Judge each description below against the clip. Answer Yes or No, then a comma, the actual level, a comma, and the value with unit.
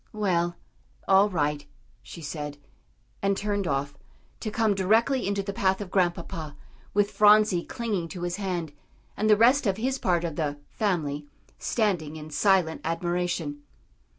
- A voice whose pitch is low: No, medium, 185 Hz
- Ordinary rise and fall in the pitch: Yes, average, 4.3 semitones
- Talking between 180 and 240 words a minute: No, average, 150 wpm